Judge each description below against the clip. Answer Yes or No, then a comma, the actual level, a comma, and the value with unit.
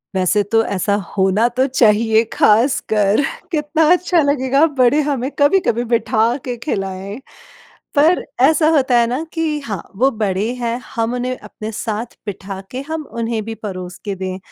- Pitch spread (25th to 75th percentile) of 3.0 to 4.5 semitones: No, average, 5.2 semitones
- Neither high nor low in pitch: No, high, 235 Hz